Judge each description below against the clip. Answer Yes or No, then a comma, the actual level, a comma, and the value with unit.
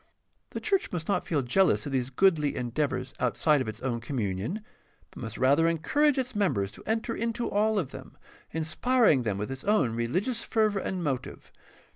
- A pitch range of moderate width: No, wide, 9.0 semitones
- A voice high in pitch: No, medium, 155 Hz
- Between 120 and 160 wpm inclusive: No, average, 180 wpm